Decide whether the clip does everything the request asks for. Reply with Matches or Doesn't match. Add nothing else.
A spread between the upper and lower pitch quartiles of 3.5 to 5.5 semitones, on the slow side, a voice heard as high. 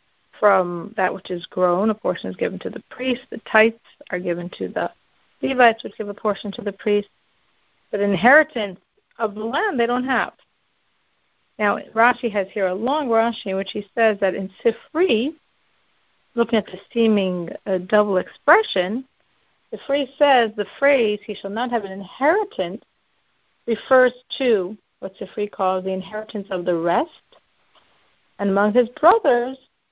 Doesn't match